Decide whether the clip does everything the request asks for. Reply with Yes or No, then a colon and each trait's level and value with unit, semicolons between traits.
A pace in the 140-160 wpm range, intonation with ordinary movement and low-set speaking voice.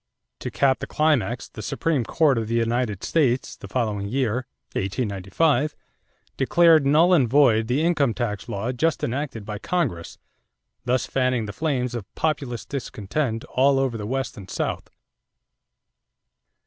Yes: average, 145 wpm; average, 4.4 semitones; low, 125 Hz